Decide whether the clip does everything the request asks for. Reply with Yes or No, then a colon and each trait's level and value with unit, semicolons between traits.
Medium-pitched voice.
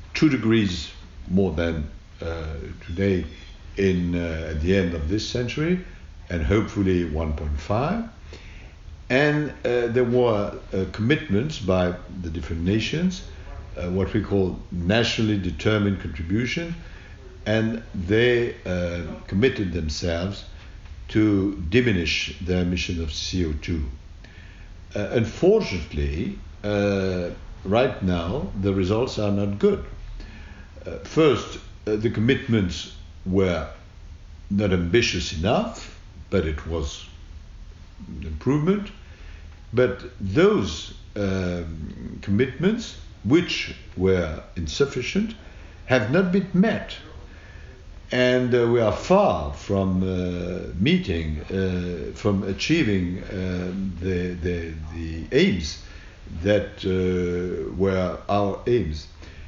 No: very low, 95 Hz